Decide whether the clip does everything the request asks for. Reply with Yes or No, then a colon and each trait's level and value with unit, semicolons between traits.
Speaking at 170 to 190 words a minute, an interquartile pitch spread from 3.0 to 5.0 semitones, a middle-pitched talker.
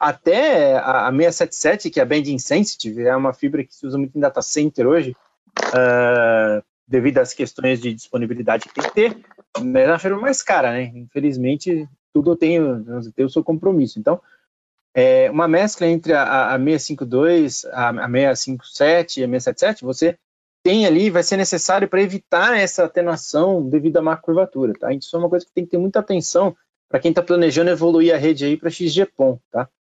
No: fast, 185 wpm; wide, 5.6 semitones; medium, 165 Hz